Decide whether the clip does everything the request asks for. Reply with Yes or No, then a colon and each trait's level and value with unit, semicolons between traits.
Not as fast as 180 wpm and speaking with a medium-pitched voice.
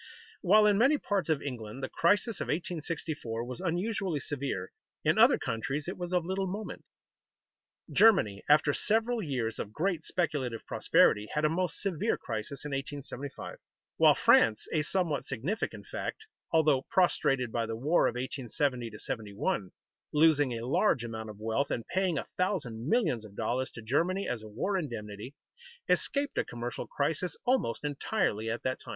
Yes: average, 160 wpm; medium, 145 Hz